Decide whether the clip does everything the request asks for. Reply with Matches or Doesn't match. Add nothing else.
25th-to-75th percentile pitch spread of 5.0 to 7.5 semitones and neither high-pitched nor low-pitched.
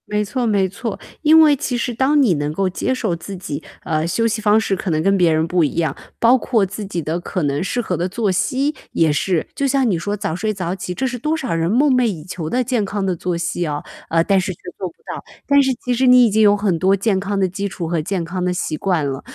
Doesn't match